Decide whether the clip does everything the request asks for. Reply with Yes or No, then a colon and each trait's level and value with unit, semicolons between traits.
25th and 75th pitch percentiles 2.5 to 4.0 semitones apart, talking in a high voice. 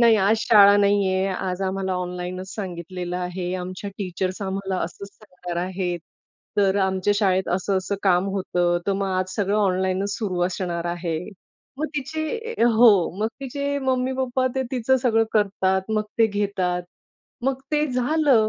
Yes: average, 3.5 semitones; high, 195 Hz